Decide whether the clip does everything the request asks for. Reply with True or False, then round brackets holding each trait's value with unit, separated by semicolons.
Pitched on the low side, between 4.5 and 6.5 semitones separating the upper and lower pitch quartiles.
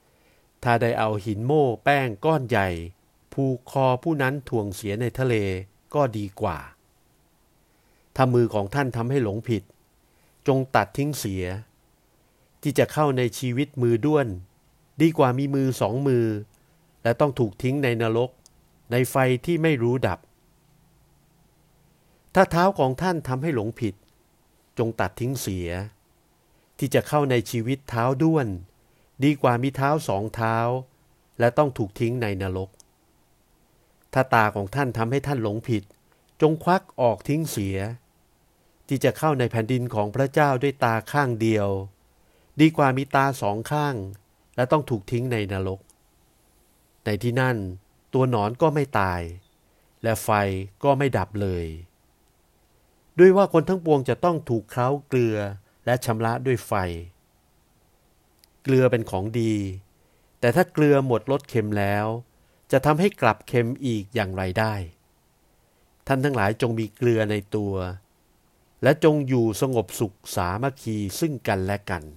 True (120 Hz; 5.1 semitones)